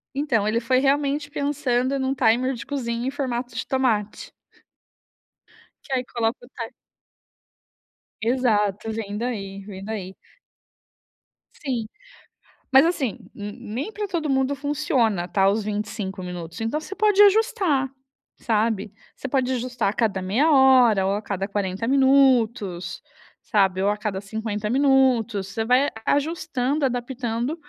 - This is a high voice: Yes, high, 240 Hz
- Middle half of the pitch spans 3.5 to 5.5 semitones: Yes, average, 4.6 semitones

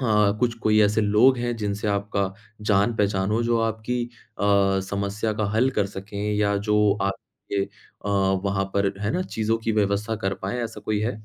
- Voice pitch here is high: No, low, 105 Hz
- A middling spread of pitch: No, narrow, 2.1 semitones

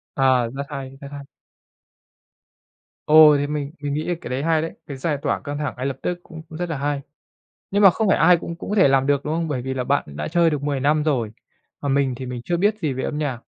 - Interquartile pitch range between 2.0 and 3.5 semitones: Yes, average, 3.1 semitones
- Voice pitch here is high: No, medium, 145 Hz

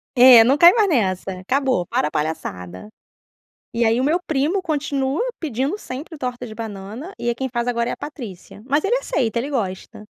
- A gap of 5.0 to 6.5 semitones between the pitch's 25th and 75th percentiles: Yes, average, 5.3 semitones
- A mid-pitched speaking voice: No, very high, 250 Hz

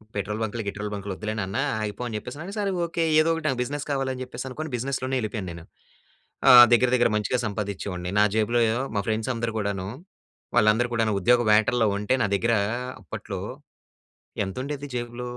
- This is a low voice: Yes, low, 115 Hz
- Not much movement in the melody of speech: No, average, 3.5 semitones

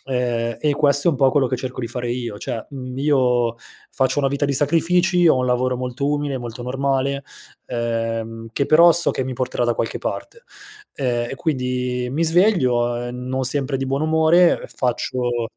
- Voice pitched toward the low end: Yes, low, 130 Hz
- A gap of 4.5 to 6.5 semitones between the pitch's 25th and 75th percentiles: No, average, 2.9 semitones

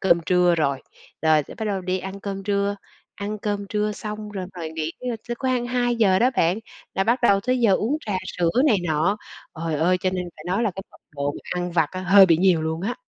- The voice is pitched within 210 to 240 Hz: No, high, 195 Hz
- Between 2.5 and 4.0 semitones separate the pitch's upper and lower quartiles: Yes, average, 3.7 semitones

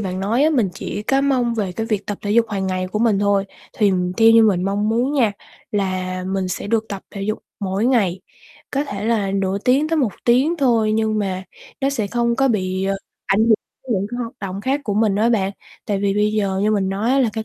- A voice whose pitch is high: Yes, high, 210 Hz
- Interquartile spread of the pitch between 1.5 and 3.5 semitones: Yes, average, 3.2 semitones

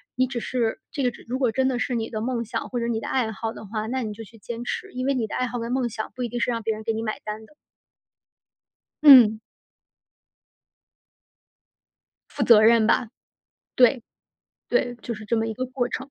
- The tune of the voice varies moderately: No, narrow, 2.2 semitones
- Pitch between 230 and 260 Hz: Yes, high, 235 Hz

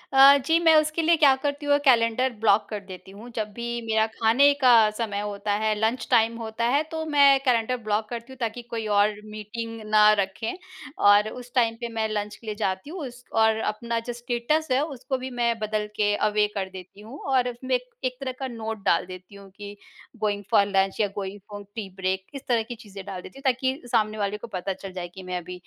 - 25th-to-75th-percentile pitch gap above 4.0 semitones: No, average, 3.5 semitones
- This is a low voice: No, high, 220 Hz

